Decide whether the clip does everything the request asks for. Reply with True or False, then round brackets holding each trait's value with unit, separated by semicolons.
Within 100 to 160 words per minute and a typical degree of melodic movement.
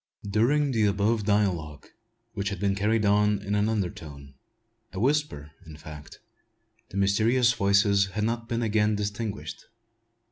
False (140 wpm; 2.2 semitones)